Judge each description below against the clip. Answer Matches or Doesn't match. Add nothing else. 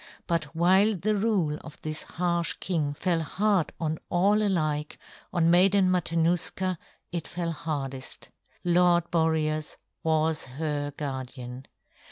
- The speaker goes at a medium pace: Doesn't match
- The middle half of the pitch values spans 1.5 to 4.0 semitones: Matches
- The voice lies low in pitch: Doesn't match